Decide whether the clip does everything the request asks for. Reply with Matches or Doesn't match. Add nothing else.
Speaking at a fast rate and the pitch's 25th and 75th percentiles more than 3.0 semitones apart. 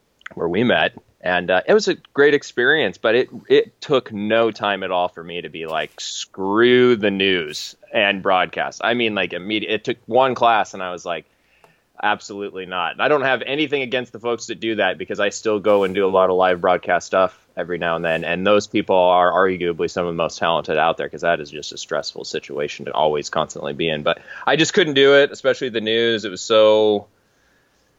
Matches